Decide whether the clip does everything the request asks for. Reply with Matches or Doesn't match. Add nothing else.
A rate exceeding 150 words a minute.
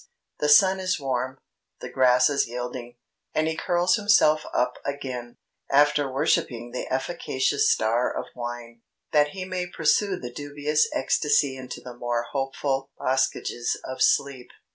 Doesn't match